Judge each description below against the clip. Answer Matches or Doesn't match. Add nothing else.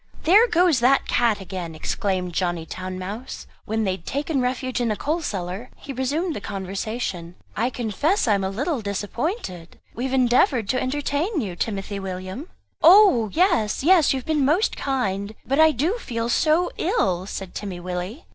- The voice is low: Doesn't match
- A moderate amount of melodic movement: Doesn't match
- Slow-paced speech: Doesn't match